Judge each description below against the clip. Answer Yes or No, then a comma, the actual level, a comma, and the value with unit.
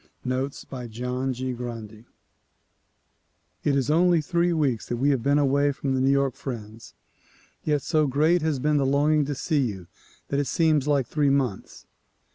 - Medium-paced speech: Yes, average, 175 wpm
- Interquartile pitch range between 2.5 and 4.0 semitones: Yes, average, 2.9 semitones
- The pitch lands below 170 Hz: Yes, medium, 140 Hz